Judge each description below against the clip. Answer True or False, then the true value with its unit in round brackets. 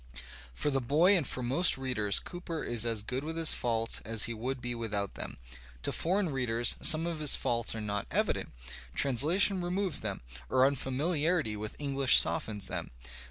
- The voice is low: True (130 Hz)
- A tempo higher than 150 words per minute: True (175 wpm)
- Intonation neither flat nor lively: False (6.1 semitones)